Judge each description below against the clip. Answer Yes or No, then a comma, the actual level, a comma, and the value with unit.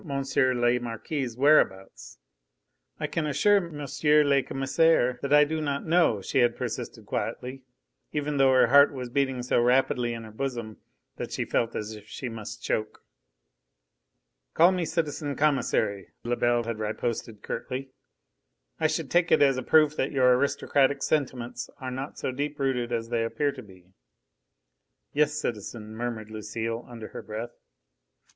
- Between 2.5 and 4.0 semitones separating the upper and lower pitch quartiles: Yes, average, 3.7 semitones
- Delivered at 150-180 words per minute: Yes, average, 155 wpm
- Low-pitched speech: Yes, low, 130 Hz